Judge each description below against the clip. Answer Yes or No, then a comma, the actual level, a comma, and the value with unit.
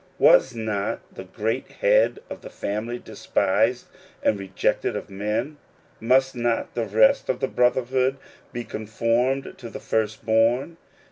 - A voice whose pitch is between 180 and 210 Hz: No, low, 115 Hz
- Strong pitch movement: No, average, 3.2 semitones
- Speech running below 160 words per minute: Yes, average, 140 wpm